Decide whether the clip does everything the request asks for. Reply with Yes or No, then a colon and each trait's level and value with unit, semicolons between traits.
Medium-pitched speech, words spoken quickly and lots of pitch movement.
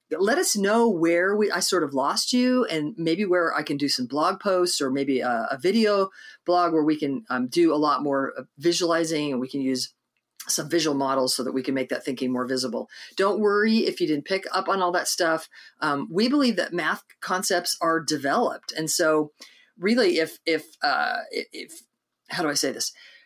Yes: medium, 165 Hz; fast, 210 wpm; wide, 6.4 semitones